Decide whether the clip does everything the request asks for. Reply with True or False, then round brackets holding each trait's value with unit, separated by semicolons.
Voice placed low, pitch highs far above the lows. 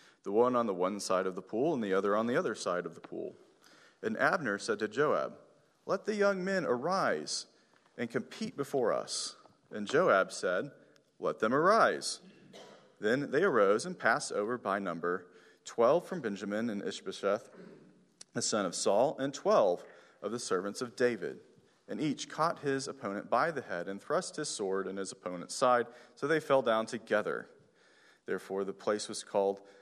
True (110 Hz; 5.8 semitones)